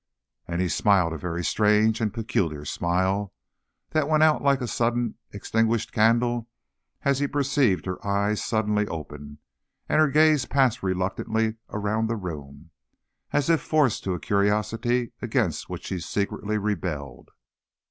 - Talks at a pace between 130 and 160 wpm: Yes, average, 145 wpm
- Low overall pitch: Yes, low, 105 Hz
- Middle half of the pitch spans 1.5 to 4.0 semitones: No, average, 4.6 semitones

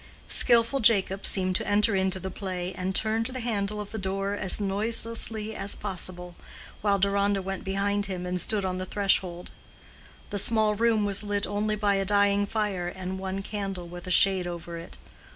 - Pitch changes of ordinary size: No, narrow, 1.9 semitones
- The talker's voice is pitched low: No, high, 200 Hz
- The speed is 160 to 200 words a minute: Yes, average, 185 wpm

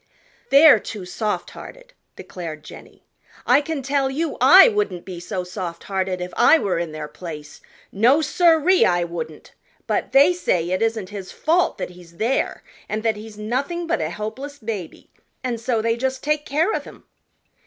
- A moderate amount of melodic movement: No, wide, 8.1 semitones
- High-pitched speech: Yes, high, 220 Hz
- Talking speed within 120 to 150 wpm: No, average, 180 wpm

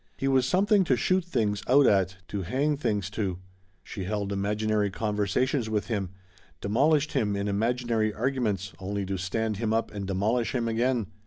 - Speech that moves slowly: No, average, 170 wpm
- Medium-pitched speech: No, low, 110 Hz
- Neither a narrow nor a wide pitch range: Yes, average, 3.9 semitones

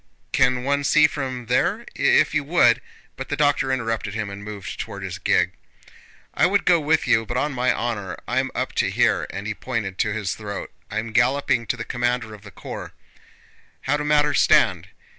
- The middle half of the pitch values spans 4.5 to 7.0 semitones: Yes, average, 4.8 semitones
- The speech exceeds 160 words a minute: Yes, average, 190 wpm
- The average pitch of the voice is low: Yes, low, 120 Hz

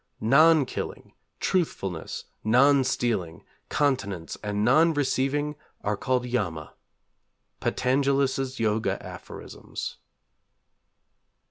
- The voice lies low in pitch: Yes, low, 130 Hz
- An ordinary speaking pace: No, slow, 85 wpm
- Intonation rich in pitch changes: No, average, 4.9 semitones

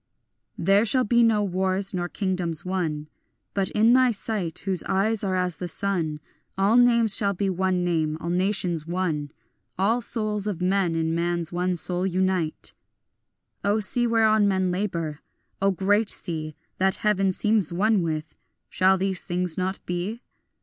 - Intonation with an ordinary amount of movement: Yes, average, 3.0 semitones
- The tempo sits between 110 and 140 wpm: No, average, 160 wpm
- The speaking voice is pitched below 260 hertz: Yes, high, 190 Hz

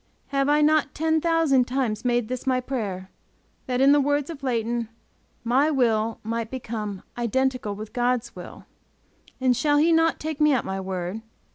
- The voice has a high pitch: Yes, very high, 255 Hz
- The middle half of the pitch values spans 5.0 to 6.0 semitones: No, average, 4.3 semitones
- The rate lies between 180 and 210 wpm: No, average, 170 wpm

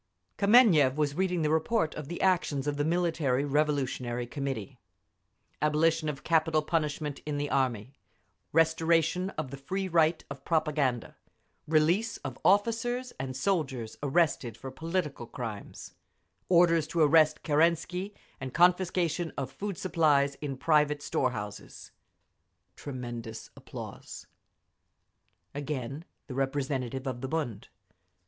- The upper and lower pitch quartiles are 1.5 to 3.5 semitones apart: No, average, 3.9 semitones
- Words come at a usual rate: No, slow, 120 wpm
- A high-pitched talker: No, medium, 150 Hz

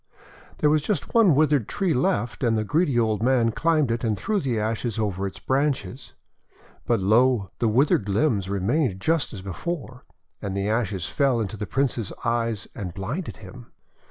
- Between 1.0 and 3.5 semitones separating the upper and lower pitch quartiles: No, average, 5.1 semitones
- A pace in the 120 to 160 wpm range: No, average, 175 wpm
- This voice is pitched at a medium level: No, low, 115 Hz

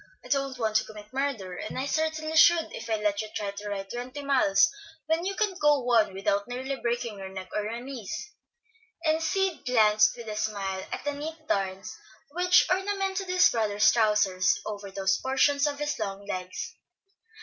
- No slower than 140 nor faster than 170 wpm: No, average, 185 wpm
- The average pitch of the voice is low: No, high, 235 Hz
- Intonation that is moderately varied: No, wide, 6.4 semitones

